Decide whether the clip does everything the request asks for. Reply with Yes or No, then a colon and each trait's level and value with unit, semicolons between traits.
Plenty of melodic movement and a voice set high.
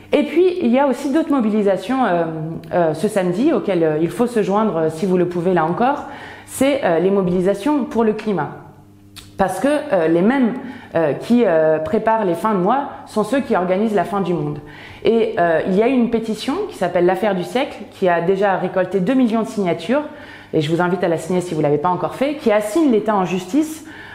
Yes: wide, 6.5 semitones; high, 200 Hz